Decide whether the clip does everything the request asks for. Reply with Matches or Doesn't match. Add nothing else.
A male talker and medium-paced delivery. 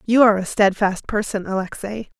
Doesn't match